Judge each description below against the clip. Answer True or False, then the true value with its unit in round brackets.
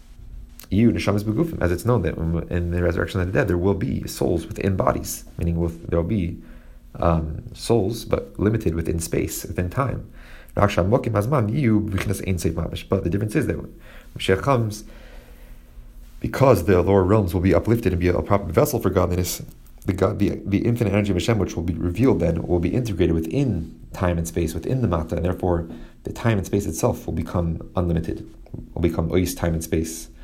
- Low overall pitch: True (90 Hz)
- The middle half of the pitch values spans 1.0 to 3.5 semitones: False (4.3 semitones)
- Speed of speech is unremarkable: True (175 wpm)